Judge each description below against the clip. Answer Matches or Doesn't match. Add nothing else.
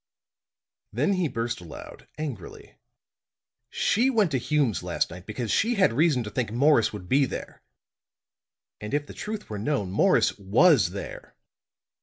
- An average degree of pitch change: Doesn't match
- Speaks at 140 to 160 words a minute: Matches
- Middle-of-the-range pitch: Doesn't match